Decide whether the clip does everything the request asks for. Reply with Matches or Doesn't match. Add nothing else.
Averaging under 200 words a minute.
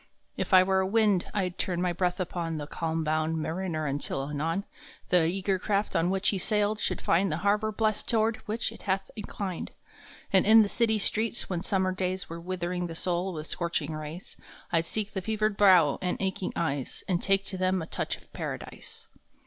Doesn't match